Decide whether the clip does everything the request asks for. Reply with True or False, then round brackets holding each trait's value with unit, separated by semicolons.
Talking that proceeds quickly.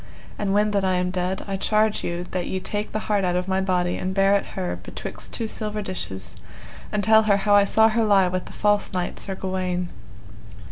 True (225 wpm)